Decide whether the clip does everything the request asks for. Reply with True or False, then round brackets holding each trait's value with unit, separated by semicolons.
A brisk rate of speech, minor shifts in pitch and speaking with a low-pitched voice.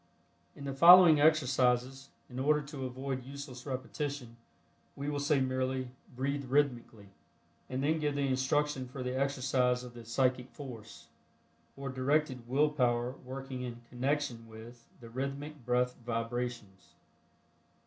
False (135 wpm; 2.3 semitones; 130 Hz)